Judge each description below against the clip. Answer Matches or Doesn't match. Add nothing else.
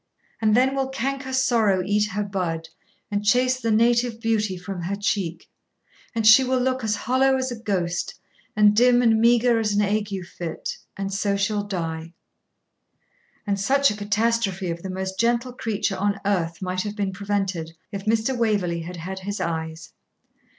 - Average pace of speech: Matches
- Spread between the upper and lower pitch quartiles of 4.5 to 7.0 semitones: Doesn't match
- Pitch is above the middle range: Matches